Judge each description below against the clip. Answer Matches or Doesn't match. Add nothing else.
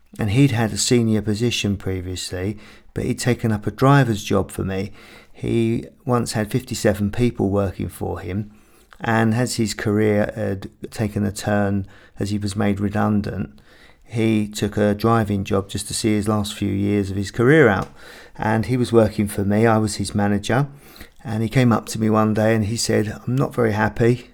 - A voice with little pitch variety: Matches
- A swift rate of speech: Doesn't match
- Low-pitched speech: Matches